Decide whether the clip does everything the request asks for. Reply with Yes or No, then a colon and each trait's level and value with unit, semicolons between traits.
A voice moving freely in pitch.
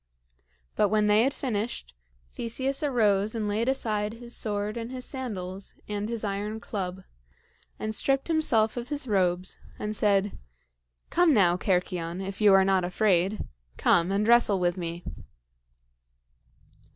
No: average, 3.5 semitones